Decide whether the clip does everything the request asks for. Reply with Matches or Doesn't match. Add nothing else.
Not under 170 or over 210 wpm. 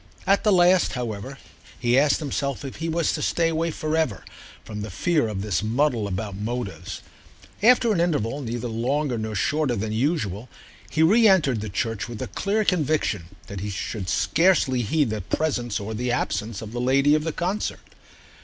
Matches